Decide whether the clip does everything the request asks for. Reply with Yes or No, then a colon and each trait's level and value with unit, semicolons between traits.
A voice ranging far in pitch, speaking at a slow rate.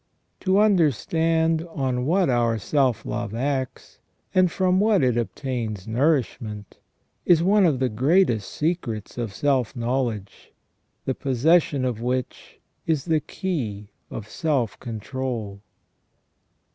Yes: wide, 5.8 semitones; slow, 120 wpm